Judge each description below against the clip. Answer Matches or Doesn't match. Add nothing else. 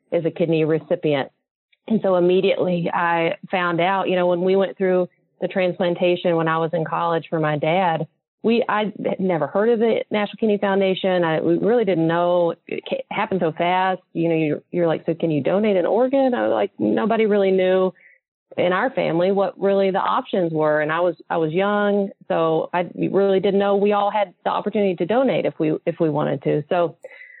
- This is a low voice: Doesn't match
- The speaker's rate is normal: Doesn't match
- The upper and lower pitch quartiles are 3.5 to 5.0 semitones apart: Doesn't match